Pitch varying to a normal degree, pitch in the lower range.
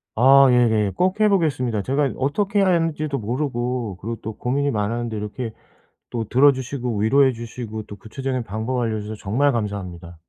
Yes: average, 4.1 semitones; low, 125 Hz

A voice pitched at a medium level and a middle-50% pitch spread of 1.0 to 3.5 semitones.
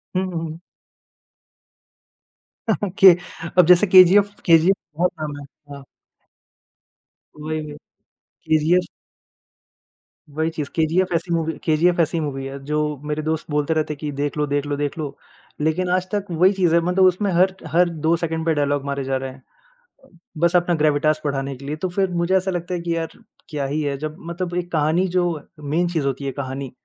Yes: medium, 160 Hz; average, 3.2 semitones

